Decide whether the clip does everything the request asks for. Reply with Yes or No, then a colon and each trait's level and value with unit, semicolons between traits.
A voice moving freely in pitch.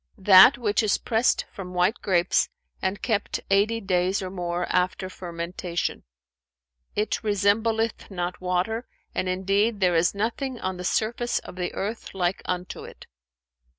No: average, 3.1 semitones